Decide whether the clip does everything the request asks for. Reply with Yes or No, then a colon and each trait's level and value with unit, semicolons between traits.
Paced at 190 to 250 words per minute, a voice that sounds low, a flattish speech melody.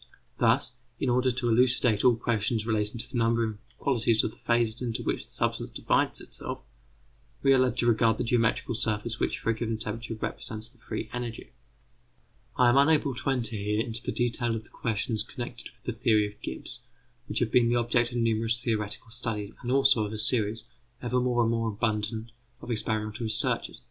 Yes: average, 200 wpm; low, 115 Hz; narrow, 1.8 semitones